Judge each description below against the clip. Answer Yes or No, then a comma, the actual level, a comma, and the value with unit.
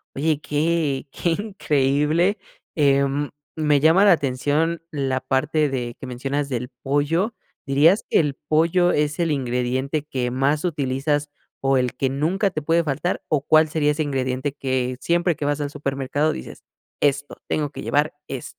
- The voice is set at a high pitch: No, medium, 145 Hz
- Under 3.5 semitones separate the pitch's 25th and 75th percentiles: Yes, average, 2.7 semitones